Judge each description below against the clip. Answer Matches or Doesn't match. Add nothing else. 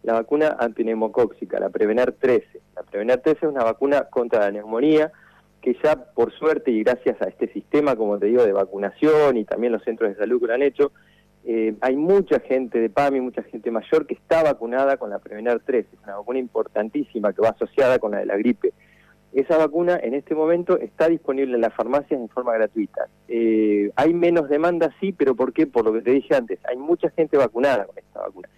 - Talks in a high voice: Doesn't match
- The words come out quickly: Matches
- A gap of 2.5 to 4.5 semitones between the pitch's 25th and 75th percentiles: Doesn't match